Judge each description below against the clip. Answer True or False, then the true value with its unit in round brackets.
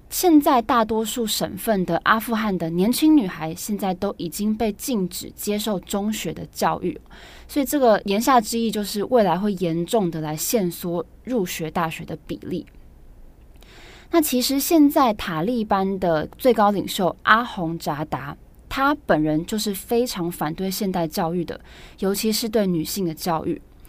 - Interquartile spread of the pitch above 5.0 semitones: True (5.4 semitones)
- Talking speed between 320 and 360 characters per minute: False (245 characters per minute)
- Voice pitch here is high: True (200 Hz)